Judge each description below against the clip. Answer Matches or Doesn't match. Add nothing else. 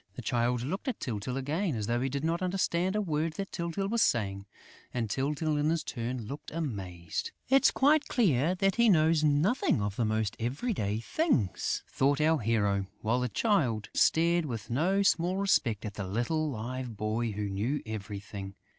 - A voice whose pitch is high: Doesn't match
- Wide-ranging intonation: Matches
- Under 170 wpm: Doesn't match